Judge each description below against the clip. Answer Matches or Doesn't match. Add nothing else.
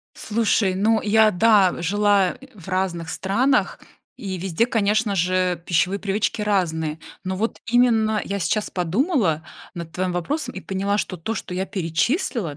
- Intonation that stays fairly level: Doesn't match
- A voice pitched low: Doesn't match